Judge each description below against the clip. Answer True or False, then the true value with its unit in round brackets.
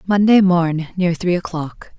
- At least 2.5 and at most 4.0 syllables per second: True (3.9 syllables/s)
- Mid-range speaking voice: True (175 Hz)